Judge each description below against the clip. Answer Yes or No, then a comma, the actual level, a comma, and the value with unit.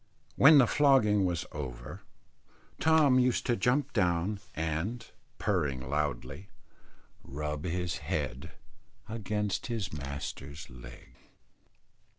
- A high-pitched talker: No, very low, 90 Hz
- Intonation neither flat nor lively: No, wide, 8.1 semitones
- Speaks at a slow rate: Yes, slow, 100 wpm